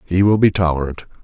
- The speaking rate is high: No, average, 195 wpm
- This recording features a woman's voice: No, male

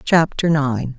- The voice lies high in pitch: No, medium, 145 Hz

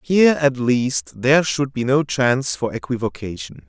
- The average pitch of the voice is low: Yes, low, 130 Hz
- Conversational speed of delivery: Yes, average, 165 wpm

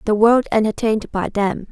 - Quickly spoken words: No, average, 175 wpm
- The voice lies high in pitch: Yes, high, 215 Hz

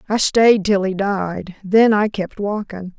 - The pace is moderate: Yes, average, 180 wpm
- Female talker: Yes, female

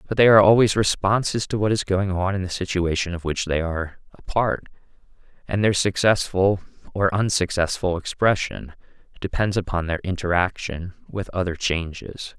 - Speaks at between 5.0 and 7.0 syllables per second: Yes, 5.1 syllables/s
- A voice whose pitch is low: Yes, very low, 95 Hz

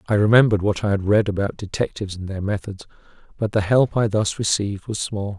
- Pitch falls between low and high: No, low, 100 Hz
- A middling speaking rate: No, fast, 210 wpm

